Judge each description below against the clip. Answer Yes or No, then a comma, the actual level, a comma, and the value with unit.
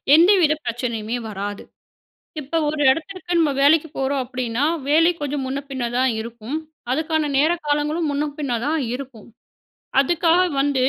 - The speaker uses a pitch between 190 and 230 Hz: No, very high, 285 Hz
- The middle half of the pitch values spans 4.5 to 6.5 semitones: No, average, 3.8 semitones